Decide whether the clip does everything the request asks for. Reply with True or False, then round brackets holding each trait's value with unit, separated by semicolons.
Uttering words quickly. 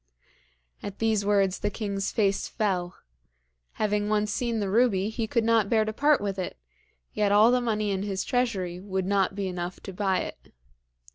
False (185 wpm)